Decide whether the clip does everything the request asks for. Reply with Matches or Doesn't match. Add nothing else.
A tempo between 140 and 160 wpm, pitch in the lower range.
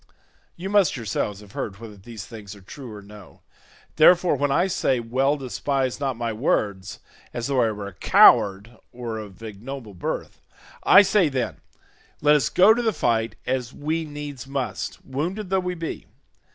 Doesn't match